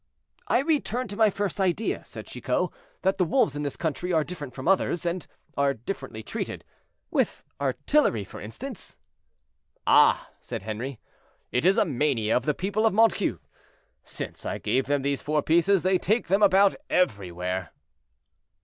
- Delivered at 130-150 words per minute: No, average, 160 wpm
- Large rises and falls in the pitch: Yes, wide, 6.9 semitones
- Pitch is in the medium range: Yes, medium, 170 Hz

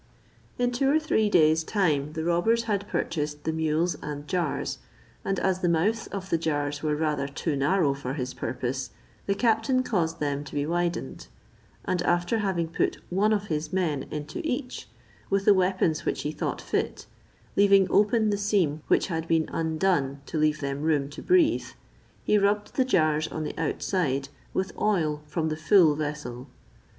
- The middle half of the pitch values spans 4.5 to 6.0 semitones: Yes, average, 5.0 semitones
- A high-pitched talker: No, medium, 165 Hz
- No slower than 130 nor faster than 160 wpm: No, average, 175 wpm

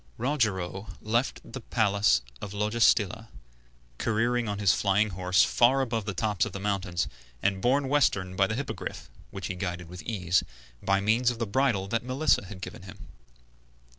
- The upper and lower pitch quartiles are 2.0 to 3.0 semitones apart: No, average, 3.5 semitones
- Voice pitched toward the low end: Yes, low, 105 Hz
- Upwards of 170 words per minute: No, average, 165 wpm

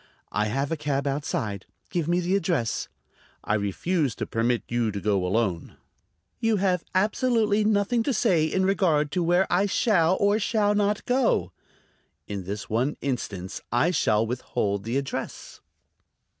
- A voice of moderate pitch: Yes, medium, 155 Hz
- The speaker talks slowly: No, average, 155 wpm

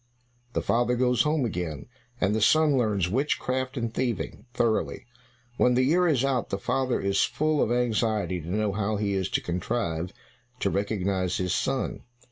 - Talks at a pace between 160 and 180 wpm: Yes, average, 170 wpm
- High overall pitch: No, low, 115 Hz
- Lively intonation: No, average, 4.7 semitones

